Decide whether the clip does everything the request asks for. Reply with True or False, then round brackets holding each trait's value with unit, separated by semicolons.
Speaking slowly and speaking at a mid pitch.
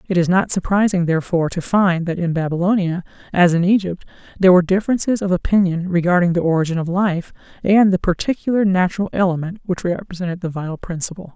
False (175 wpm; 180 Hz)